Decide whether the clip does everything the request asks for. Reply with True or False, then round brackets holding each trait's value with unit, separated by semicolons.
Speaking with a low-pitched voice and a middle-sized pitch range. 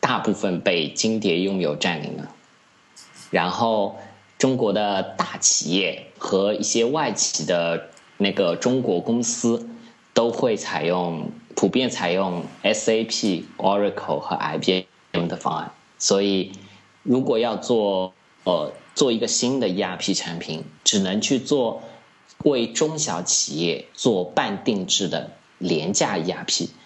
True (100 Hz; 4.1 semitones)